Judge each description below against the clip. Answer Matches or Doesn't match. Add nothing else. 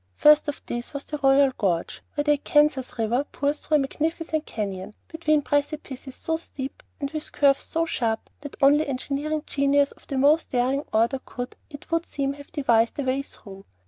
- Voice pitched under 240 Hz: Doesn't match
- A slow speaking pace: Doesn't match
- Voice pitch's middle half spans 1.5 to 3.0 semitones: Matches